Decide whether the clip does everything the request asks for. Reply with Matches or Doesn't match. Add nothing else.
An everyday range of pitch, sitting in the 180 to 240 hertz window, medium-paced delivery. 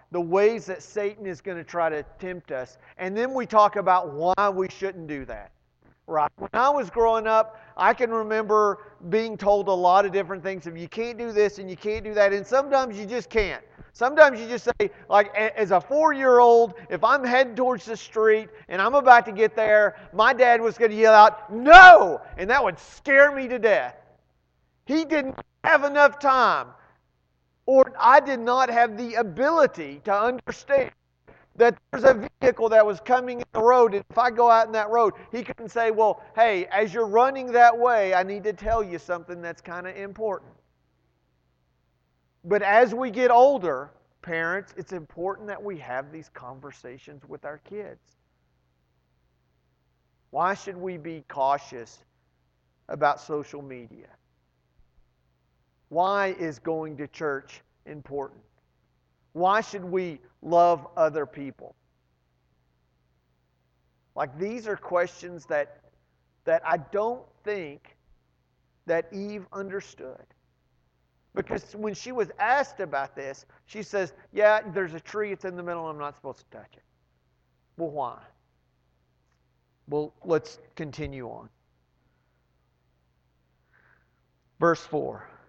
Doesn't match